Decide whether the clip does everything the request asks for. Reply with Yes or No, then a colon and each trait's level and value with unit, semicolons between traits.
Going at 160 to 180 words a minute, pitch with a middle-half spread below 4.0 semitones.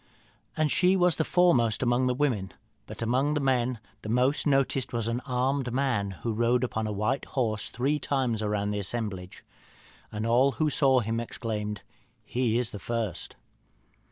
Yes: average, 170 wpm; average, 3.6 semitones